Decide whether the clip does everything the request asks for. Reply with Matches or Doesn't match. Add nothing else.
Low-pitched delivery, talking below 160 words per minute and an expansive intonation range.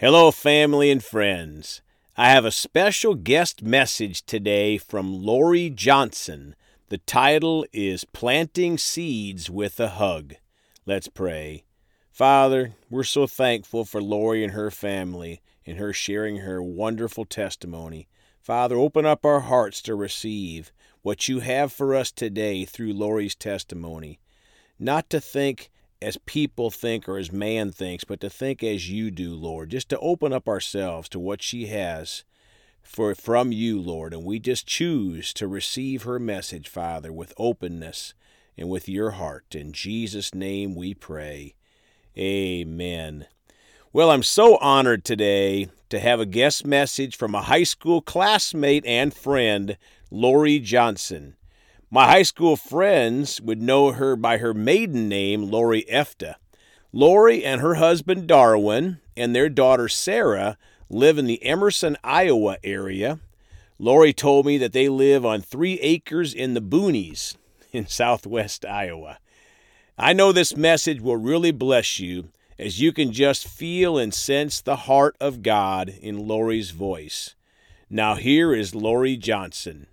Matches